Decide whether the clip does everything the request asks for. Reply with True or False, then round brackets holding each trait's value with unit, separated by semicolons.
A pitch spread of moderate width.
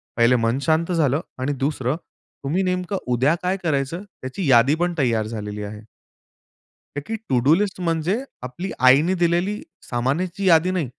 False (6.0 semitones)